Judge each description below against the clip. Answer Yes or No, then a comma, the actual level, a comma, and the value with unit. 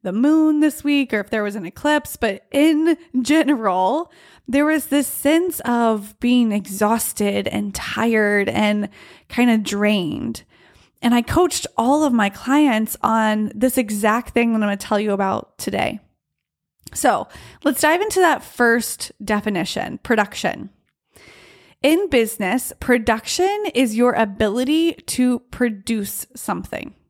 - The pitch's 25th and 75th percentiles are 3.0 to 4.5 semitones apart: No, wide, 5.5 semitones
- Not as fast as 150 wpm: Yes, slow, 135 wpm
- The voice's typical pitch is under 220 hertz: No, high, 240 Hz